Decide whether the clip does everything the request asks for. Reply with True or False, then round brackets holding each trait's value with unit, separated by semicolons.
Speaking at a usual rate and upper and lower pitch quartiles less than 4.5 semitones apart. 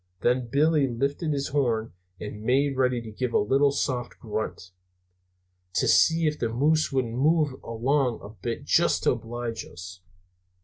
True (160 wpm; 3.6 semitones)